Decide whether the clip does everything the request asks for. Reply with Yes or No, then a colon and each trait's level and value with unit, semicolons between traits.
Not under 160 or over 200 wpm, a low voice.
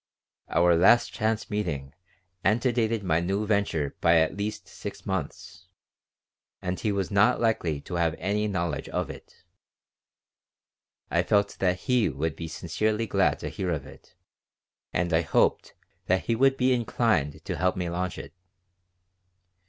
No: average, 150 wpm; very low, 95 Hz